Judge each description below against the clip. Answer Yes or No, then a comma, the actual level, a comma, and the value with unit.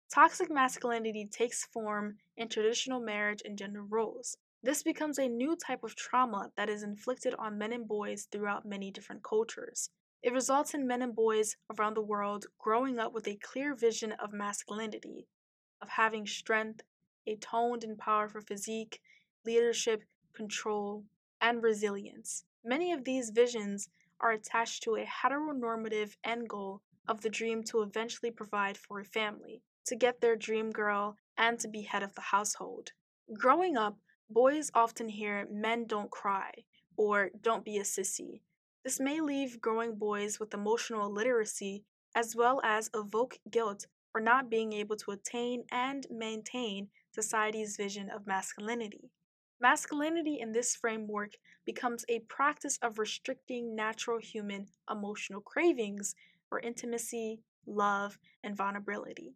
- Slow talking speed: No, average, 145 wpm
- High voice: Yes, high, 220 Hz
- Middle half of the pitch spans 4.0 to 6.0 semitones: No, narrow, 2.5 semitones